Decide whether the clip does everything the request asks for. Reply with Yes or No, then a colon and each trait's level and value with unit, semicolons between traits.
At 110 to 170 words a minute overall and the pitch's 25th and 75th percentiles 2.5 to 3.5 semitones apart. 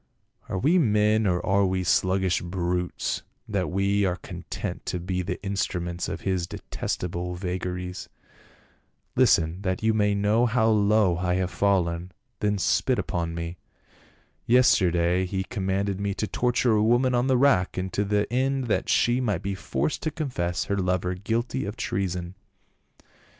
Yes: average, 160 wpm; average, 3.1 semitones